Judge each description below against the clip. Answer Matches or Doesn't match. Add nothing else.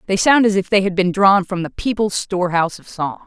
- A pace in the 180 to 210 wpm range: Doesn't match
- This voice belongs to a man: Doesn't match